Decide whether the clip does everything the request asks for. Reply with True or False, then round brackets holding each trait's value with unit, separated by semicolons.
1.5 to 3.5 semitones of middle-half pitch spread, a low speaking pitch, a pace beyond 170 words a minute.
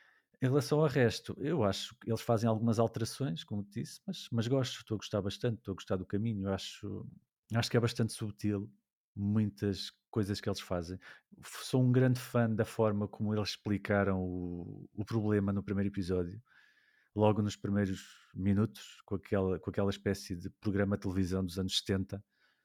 True (2.8 semitones; 105 Hz; 180 wpm)